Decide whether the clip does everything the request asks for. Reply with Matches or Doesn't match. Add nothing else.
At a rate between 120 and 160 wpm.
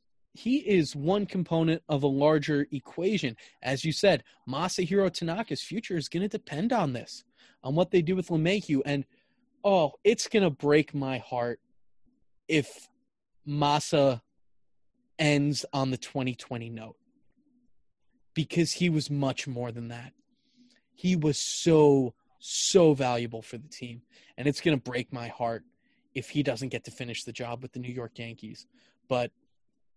Matches